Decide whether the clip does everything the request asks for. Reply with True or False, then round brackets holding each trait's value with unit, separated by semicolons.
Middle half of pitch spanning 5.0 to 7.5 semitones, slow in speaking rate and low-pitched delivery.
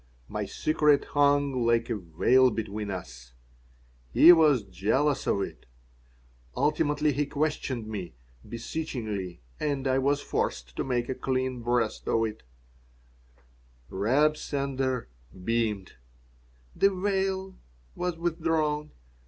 True (5.4 semitones; 110 wpm; 130 Hz)